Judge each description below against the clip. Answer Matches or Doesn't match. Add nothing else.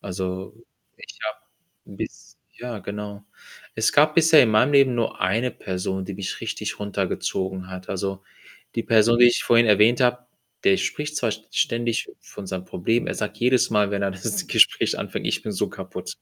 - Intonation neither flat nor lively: Matches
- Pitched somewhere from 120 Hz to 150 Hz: Doesn't match